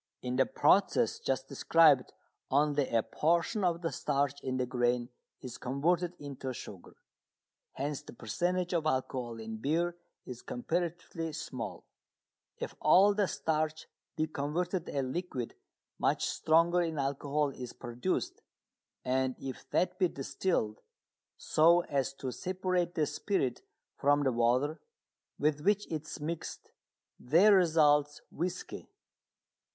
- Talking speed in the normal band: No, slow, 130 wpm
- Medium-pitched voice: Yes, medium, 150 Hz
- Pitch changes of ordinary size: Yes, average, 4.7 semitones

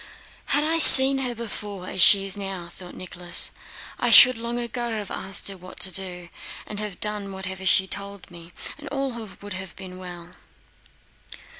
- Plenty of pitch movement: No, average, 4.1 semitones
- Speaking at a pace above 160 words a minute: Yes, average, 175 wpm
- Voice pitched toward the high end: Yes, high, 195 Hz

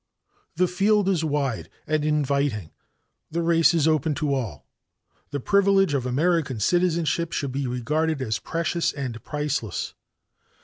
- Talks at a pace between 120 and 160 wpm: Yes, slow, 135 wpm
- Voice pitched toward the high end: No, medium, 150 Hz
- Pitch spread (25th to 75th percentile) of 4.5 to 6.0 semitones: No, average, 3.9 semitones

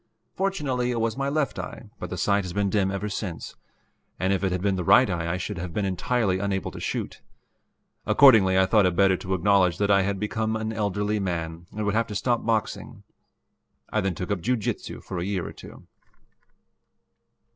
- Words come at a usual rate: No, fast, 210 wpm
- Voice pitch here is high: No, low, 100 Hz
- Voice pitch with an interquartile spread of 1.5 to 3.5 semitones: Yes, average, 2.9 semitones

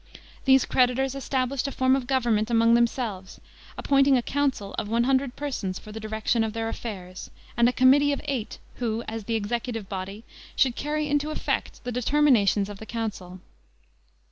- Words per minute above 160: Yes, average, 170 wpm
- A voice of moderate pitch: No, high, 235 Hz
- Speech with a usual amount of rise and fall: Yes, average, 3.7 semitones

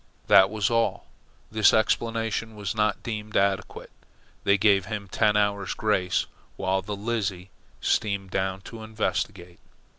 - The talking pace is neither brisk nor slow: No, slow, 130 wpm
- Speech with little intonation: Yes, narrow, 2.2 semitones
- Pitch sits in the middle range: No, low, 105 Hz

